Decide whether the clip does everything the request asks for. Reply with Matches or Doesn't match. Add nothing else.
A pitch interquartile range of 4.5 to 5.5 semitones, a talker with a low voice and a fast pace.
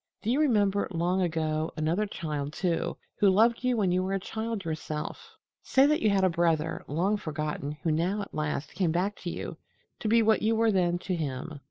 Doesn't match